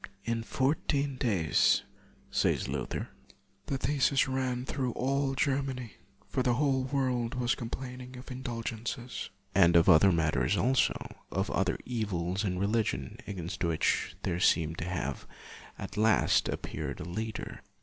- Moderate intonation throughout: No, wide, 6.1 semitones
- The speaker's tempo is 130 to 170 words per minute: Yes, average, 150 wpm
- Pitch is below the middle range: Yes, low, 120 Hz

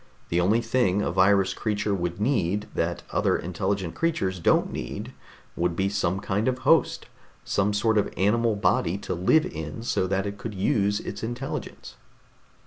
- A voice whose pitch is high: No, low, 100 Hz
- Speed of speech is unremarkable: Yes, average, 170 wpm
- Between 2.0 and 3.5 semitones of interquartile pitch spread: Yes, average, 2.8 semitones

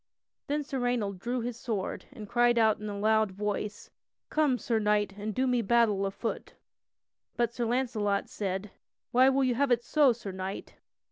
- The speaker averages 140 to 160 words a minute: No, average, 180 wpm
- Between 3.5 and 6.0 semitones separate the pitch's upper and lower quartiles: No, average, 3.1 semitones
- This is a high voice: Yes, high, 230 Hz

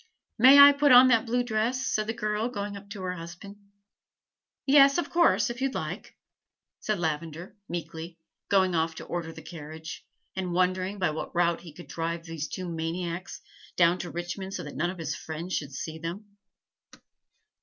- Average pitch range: Yes, average, 4.4 semitones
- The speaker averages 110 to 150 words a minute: No, average, 180 wpm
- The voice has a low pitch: No, medium, 180 Hz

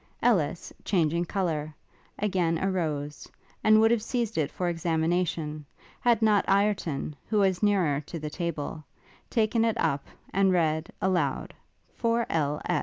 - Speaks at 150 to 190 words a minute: No, slow, 135 wpm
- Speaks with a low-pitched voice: No, medium, 175 Hz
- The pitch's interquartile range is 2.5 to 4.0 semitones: No, average, 5.0 semitones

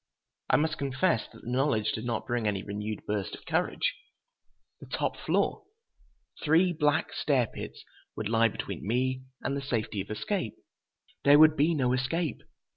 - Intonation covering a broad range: Yes, wide, 5.7 semitones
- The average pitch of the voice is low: Yes, low, 130 Hz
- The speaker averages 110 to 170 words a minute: Yes, average, 165 wpm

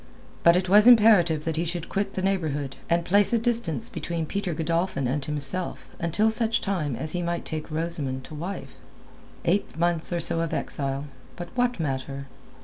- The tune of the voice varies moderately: Yes, average, 4.1 semitones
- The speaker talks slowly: No, average, 180 wpm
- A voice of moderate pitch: Yes, medium, 170 Hz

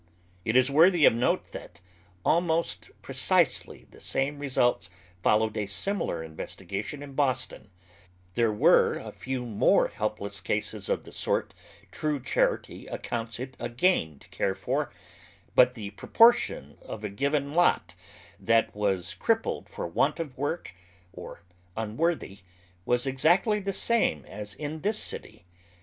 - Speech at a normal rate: Yes, average, 145 wpm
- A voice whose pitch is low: Yes, low, 130 Hz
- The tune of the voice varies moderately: No, wide, 7.0 semitones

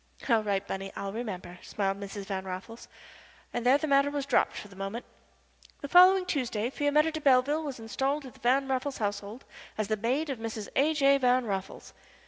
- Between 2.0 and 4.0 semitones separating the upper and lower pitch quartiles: No, wide, 5.6 semitones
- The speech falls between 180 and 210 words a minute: Yes, average, 195 wpm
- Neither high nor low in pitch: No, high, 245 Hz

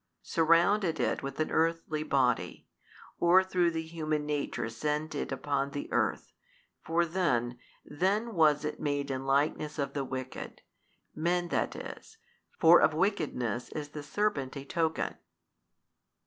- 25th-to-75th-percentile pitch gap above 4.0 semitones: No, average, 3.4 semitones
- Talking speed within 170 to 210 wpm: No, average, 140 wpm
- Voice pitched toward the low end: No, medium, 155 Hz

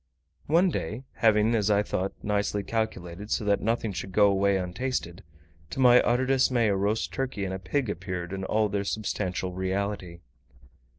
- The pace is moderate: Yes, average, 170 wpm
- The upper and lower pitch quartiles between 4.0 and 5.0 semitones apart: No, average, 3.1 semitones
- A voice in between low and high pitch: No, low, 100 Hz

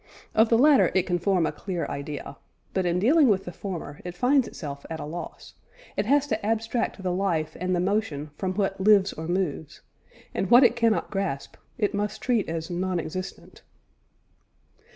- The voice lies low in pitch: No, high, 190 Hz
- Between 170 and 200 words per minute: Yes, average, 185 wpm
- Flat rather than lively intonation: No, average, 4.0 semitones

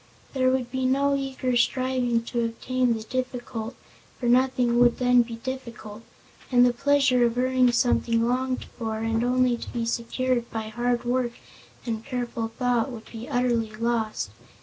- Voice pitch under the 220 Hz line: No, high, 245 Hz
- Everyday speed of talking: Yes, average, 160 wpm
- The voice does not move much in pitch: Yes, narrow, 1.8 semitones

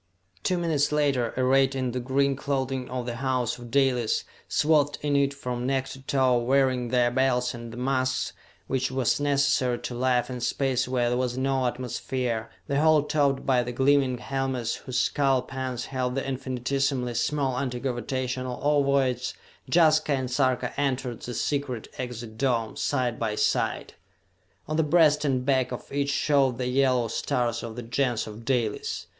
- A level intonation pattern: Yes, narrow, 2.0 semitones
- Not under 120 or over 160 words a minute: No, average, 170 wpm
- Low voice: Yes, low, 130 Hz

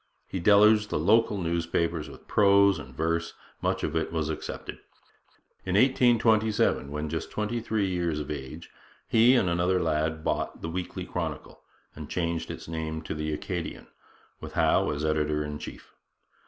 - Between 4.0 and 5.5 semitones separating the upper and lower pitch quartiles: Yes, average, 4.6 semitones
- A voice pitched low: Yes, very low, 85 Hz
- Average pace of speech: Yes, average, 160 wpm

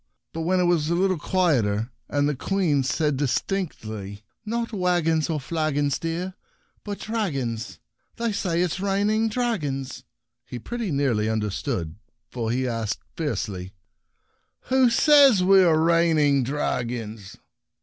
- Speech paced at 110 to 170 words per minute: Yes, average, 150 wpm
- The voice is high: No, medium, 155 Hz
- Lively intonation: Yes, wide, 7.3 semitones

